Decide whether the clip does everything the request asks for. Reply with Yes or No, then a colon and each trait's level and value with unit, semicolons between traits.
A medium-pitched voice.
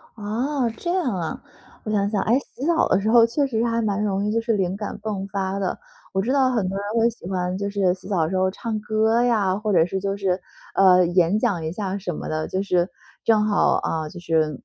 No: high, 200 Hz